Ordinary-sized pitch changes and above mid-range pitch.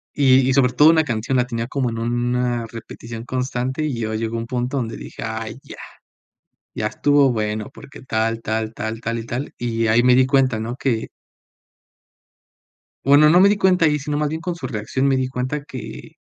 No: average, 3.3 semitones; low, 125 Hz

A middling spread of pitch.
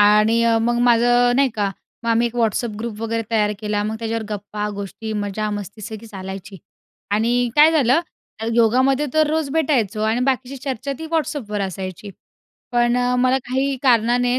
Yes: average, 3.3 semitones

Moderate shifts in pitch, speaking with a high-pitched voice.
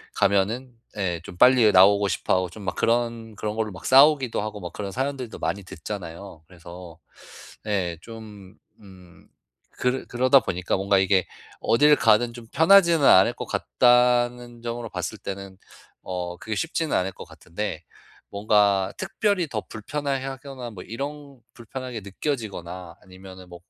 No: average, 5.0 semitones; low, 105 Hz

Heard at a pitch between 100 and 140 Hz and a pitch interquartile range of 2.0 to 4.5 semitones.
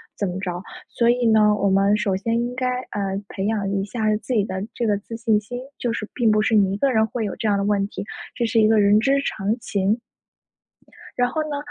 No: high, 215 Hz; average, 2.7 semitones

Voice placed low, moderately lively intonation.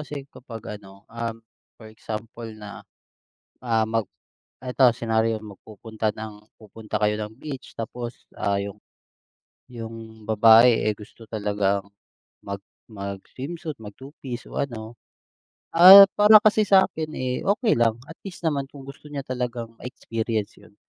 Yes: low, 115 Hz; average, 3.5 semitones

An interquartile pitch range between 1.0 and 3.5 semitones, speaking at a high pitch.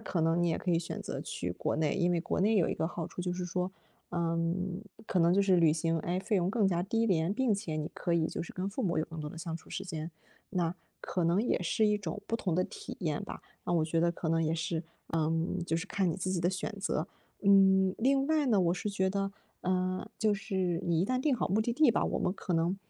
No: average, 3.0 semitones; medium, 180 Hz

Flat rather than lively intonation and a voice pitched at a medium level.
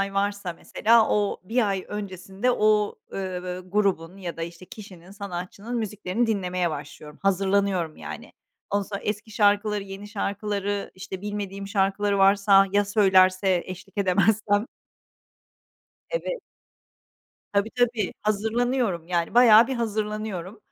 No: narrow, 2.2 semitones; high, 200 Hz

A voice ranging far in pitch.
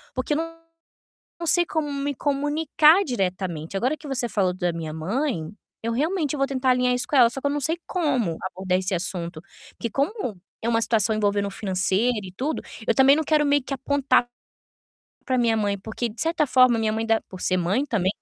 Yes: wide, 6.4 semitones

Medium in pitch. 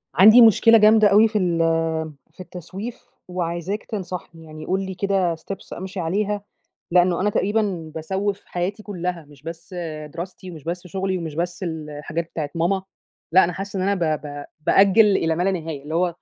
Yes: medium, 180 Hz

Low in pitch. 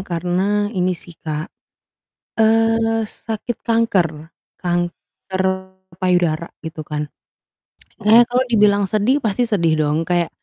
No: high, 190 Hz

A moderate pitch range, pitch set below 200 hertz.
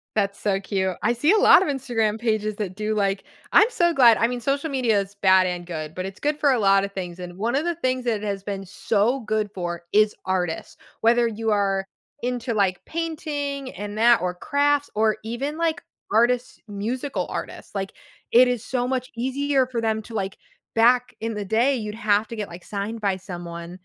No: average, 4.3 semitones; high, 220 Hz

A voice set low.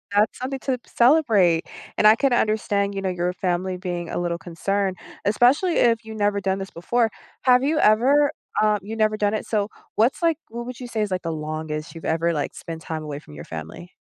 No: high, 205 Hz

